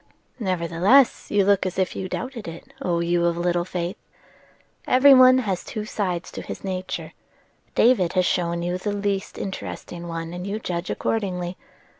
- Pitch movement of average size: Yes, average, 3.1 semitones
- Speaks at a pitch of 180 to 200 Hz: Yes, medium, 185 Hz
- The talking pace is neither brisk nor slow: Yes, average, 165 wpm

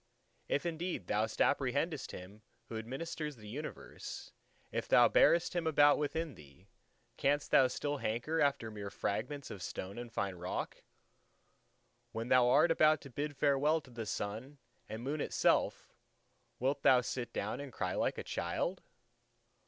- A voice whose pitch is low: Yes, low, 130 Hz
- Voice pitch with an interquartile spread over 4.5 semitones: Yes, average, 5.1 semitones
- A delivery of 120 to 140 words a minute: No, average, 150 wpm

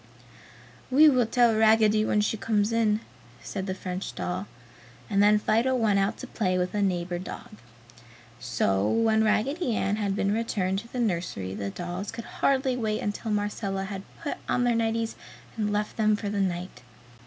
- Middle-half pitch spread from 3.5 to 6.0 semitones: No, average, 2.9 semitones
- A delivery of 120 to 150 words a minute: No, average, 175 wpm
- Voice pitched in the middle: No, high, 210 Hz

